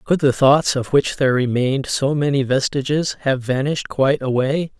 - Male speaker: Yes, male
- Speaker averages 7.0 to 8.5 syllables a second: No, 5.3 syllables/s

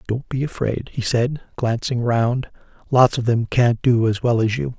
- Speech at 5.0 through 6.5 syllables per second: No, 4.4 syllables/s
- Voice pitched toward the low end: Yes, low, 120 Hz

